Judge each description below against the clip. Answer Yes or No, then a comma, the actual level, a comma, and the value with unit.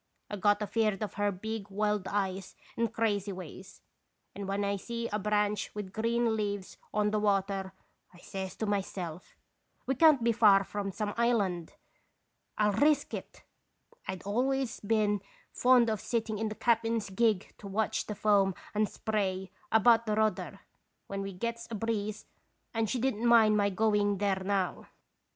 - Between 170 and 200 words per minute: Yes, average, 175 wpm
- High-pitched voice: Yes, high, 210 Hz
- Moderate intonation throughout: No, narrow, 2.3 semitones